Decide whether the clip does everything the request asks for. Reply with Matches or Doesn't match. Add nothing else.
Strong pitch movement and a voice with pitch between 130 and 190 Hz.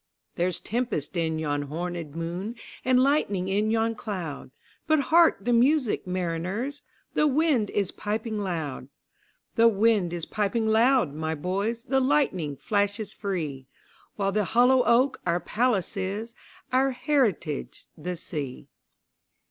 Doesn't match